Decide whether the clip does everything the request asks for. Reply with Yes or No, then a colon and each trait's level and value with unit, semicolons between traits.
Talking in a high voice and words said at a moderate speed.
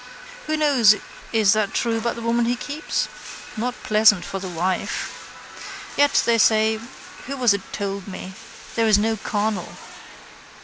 Yes: high, 220 Hz; average, 150 wpm